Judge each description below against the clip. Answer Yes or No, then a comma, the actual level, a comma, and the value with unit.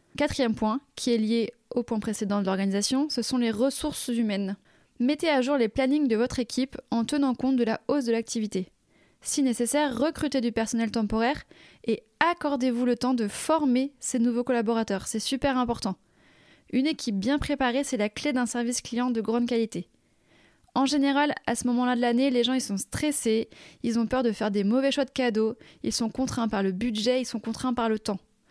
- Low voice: No, high, 245 Hz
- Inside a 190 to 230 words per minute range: Yes, average, 200 wpm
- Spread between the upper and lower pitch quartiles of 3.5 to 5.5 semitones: No, average, 2.9 semitones